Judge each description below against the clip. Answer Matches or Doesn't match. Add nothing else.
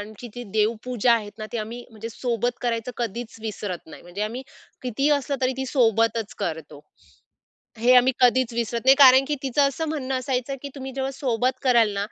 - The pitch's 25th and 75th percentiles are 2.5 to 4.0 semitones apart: Matches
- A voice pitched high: Matches